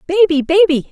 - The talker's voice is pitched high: Yes, very high, 335 Hz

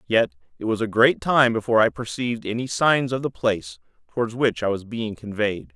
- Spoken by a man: Yes, male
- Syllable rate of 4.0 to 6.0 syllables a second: Yes, 5.6 syllables/s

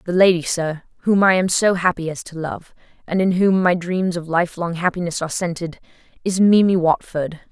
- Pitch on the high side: No, medium, 175 Hz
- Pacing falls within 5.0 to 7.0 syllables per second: Yes, 5.2 syllables/s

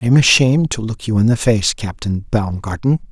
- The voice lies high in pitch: No, low, 115 Hz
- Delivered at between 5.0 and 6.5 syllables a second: Yes, 5.4 syllables/s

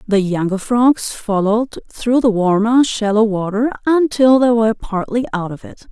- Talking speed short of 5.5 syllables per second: Yes, 4.5 syllables/s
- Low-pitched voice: No, high, 225 Hz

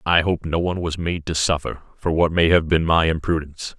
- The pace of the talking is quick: Yes, fast, 240 wpm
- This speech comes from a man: Yes, male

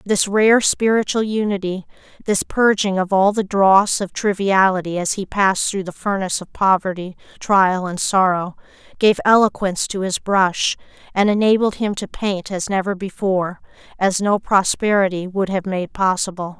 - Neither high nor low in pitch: No, high, 195 Hz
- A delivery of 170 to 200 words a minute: No, average, 150 wpm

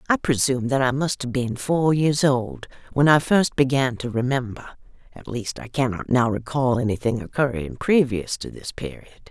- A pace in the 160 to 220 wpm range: Yes, average, 180 wpm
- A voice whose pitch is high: No, low, 130 Hz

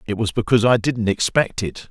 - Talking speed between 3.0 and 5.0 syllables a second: No, 5.7 syllables/s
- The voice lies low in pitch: Yes, low, 110 Hz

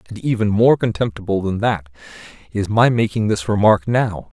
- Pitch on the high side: No, low, 105 Hz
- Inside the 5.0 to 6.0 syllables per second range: Yes, 5.1 syllables/s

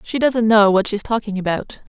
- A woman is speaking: Yes, female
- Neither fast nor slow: No, fast, 215 wpm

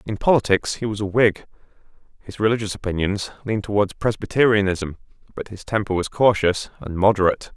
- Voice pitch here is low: Yes, low, 105 Hz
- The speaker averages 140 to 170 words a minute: Yes, average, 150 wpm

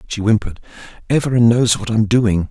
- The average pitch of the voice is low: Yes, low, 110 Hz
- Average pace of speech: Yes, average, 170 wpm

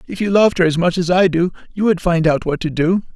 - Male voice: Yes, male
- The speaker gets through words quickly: Yes, fast, 305 wpm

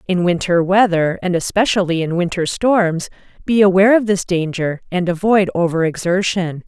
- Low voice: No, medium, 185 Hz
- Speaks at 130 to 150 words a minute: Yes, average, 145 wpm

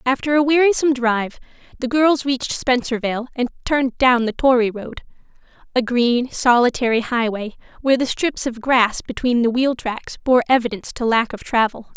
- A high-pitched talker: Yes, high, 245 Hz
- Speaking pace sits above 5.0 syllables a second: Yes, 5.4 syllables/s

